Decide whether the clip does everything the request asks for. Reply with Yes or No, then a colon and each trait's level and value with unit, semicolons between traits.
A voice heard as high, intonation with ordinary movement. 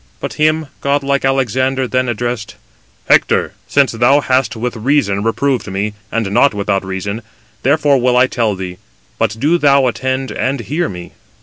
No: low, 125 Hz; average, 4.5 semitones